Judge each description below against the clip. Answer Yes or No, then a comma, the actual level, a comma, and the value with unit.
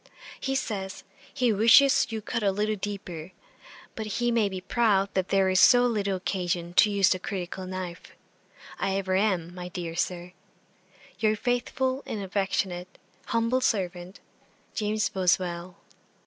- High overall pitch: Yes, high, 195 Hz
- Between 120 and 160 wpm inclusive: Yes, average, 150 wpm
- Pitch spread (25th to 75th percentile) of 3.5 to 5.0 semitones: No, average, 3.0 semitones